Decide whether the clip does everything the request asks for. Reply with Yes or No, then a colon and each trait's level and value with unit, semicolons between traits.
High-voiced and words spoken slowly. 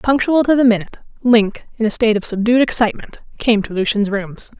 No: high, 225 Hz; average, 195 wpm